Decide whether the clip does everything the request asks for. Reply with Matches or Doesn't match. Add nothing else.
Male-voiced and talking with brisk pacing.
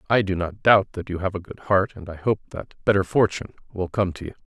Matches